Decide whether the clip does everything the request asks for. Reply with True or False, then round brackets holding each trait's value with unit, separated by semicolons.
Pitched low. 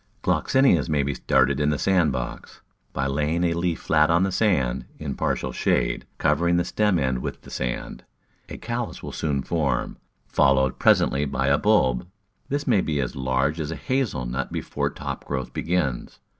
True (75 Hz)